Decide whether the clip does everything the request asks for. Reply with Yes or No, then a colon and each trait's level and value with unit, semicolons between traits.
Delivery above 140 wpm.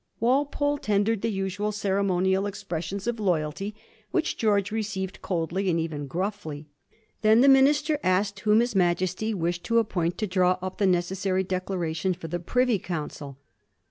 Yes: average, 155 wpm